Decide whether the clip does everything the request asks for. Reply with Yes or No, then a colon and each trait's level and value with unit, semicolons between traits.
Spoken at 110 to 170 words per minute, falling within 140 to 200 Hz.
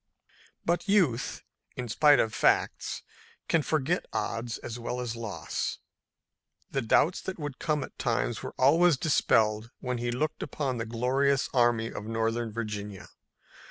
No: average, 145 wpm; low, 125 Hz